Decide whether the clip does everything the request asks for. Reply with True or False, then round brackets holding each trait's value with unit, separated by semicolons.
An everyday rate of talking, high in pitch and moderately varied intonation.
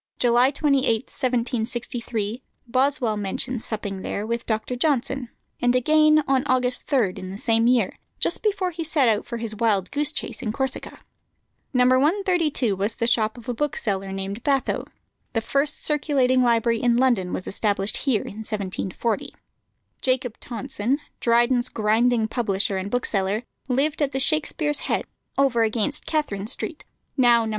True (150 wpm; 240 Hz; 3.8 semitones)